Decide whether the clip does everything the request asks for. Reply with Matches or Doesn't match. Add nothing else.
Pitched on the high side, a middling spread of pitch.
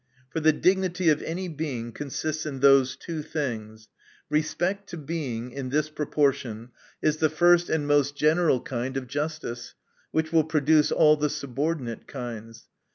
Doesn't match